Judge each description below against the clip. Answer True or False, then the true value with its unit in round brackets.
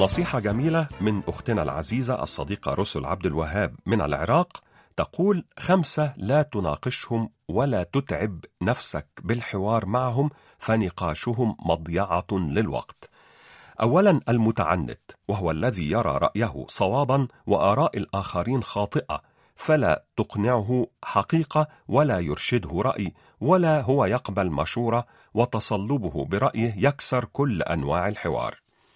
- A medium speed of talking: True (100 wpm)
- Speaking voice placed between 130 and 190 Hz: False (115 Hz)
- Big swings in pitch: True (5.9 semitones)